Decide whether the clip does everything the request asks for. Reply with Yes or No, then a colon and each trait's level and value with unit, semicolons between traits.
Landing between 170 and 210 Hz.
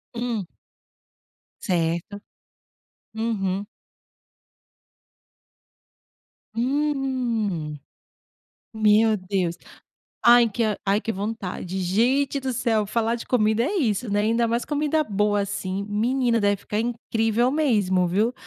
No: high, 220 Hz